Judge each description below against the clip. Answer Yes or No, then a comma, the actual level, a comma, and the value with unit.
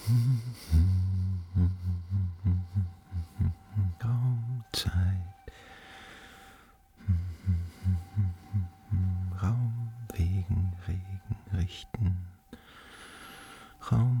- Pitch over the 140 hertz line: No, very low, 95 Hz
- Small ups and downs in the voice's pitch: No, average, 3.0 semitones